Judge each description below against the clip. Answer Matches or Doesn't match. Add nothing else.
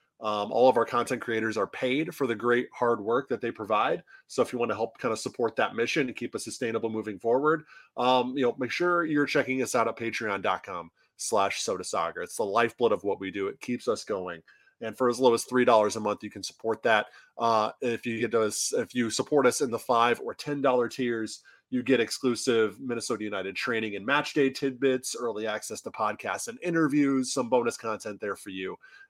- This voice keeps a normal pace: Doesn't match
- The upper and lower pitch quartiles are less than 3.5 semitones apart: Matches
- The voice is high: Doesn't match